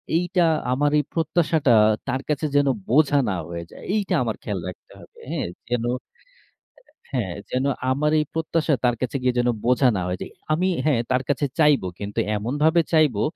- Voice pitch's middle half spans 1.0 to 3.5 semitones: No, average, 4.3 semitones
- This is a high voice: No, medium, 140 Hz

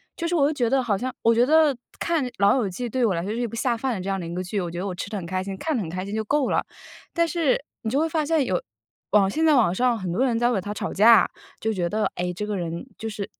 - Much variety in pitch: Yes, wide, 5.7 semitones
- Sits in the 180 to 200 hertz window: No, high, 220 Hz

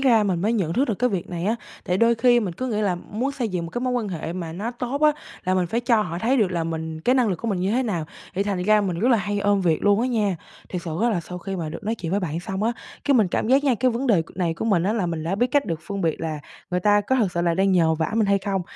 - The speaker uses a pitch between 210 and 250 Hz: No, high, 200 Hz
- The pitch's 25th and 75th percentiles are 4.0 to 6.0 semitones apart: Yes, average, 4.9 semitones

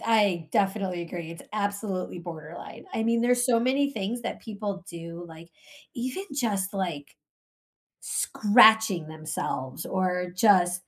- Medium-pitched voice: No, high, 195 Hz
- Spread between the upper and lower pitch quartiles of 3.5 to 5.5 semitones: Yes, average, 4.5 semitones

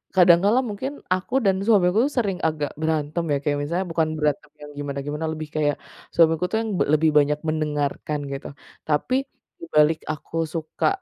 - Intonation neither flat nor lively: Yes, average, 3.5 semitones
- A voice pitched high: No, medium, 155 Hz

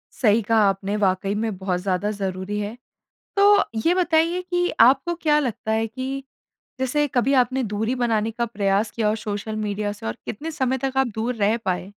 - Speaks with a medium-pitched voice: No, high, 225 Hz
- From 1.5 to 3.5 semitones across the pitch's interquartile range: No, average, 4.5 semitones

